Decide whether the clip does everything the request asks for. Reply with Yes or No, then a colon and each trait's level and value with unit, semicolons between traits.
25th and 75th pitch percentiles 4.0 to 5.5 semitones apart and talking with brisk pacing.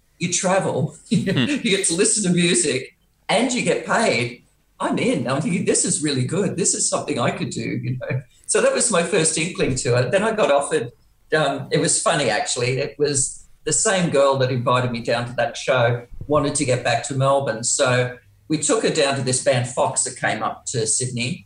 Yes: average, 4.4 semitones; fast, 215 wpm